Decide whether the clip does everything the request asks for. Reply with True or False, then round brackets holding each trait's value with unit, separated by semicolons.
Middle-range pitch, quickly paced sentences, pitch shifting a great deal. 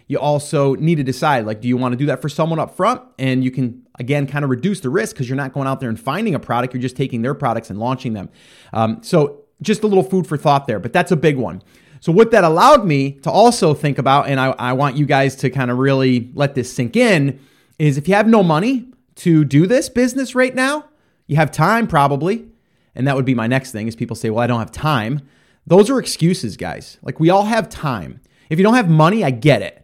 True (145 Hz; 255 wpm; 5.8 semitones)